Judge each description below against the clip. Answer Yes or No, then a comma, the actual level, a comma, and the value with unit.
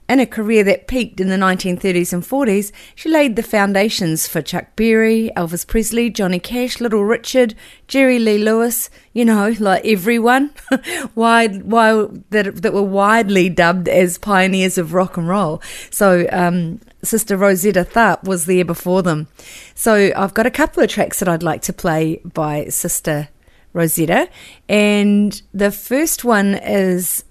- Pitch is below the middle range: No, high, 200 Hz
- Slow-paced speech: No, average, 160 wpm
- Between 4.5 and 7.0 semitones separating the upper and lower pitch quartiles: No, average, 3.9 semitones